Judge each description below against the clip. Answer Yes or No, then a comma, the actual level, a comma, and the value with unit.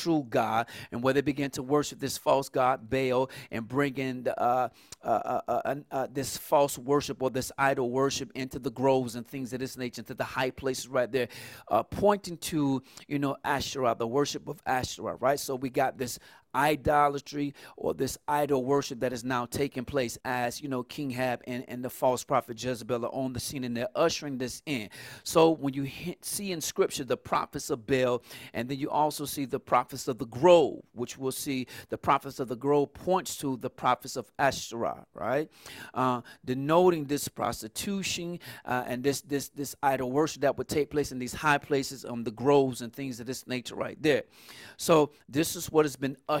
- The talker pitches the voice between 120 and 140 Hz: Yes, low, 135 Hz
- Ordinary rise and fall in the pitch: No, narrow, 2.3 semitones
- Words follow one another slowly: No, fast, 205 wpm